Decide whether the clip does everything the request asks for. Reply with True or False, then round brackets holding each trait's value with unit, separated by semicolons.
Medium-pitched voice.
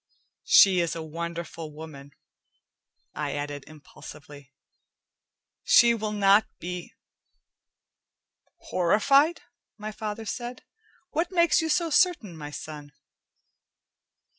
True (180 Hz)